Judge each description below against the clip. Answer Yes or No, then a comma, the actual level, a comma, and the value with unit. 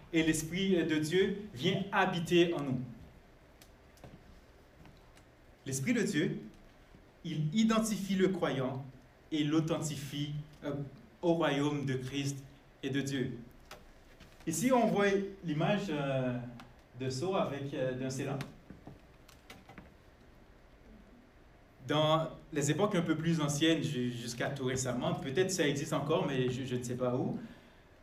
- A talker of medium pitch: Yes, medium, 145 Hz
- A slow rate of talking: Yes, slow, 120 wpm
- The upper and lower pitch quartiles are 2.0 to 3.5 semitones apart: No, average, 4.5 semitones